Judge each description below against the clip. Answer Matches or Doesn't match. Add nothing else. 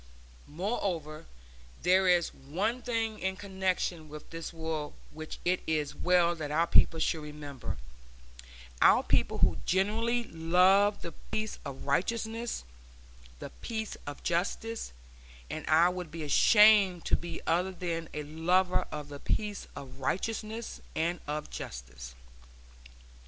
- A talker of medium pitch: Matches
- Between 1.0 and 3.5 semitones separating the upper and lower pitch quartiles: Doesn't match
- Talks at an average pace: Doesn't match